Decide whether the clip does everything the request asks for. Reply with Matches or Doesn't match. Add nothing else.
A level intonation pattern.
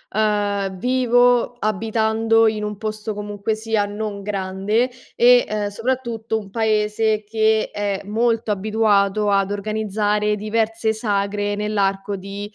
Matches